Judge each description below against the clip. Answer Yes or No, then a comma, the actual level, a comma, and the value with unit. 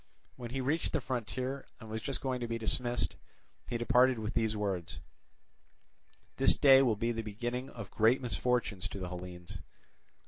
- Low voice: Yes, low, 115 Hz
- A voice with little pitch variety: No, average, 3.3 semitones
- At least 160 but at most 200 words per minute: Yes, average, 170 wpm